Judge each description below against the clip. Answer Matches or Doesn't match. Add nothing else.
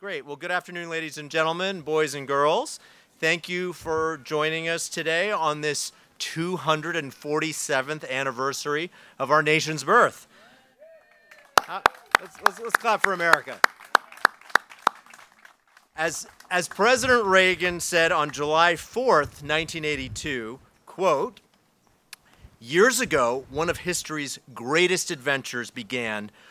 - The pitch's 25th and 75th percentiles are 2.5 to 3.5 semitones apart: Matches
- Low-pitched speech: Doesn't match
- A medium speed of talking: Doesn't match